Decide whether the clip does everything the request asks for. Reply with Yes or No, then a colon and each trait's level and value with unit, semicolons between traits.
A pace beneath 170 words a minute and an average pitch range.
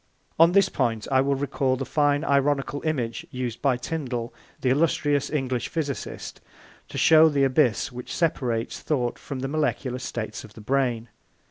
Yes: average, 160 wpm; average, 3.0 semitones